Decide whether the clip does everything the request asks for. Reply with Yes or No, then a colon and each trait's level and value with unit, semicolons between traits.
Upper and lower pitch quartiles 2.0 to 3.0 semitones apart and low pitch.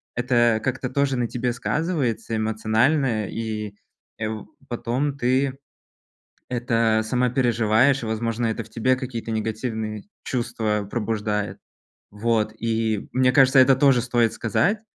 Yes: average, 2.7 semitones; low, 115 Hz